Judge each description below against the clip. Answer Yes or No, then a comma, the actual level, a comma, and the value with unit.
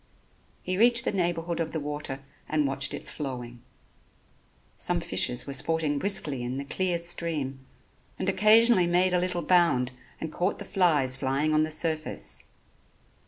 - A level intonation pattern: No, average, 4.5 semitones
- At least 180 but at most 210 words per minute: No, average, 155 wpm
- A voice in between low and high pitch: Yes, medium, 160 Hz